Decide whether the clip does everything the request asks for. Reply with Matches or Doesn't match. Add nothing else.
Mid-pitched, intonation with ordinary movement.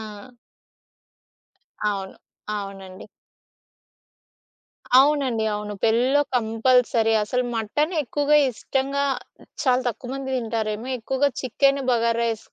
Doesn't match